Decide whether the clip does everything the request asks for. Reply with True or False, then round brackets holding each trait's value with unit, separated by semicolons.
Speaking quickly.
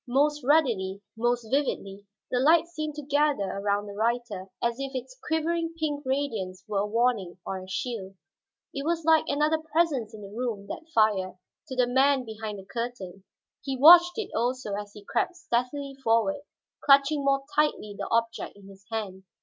False (175 wpm)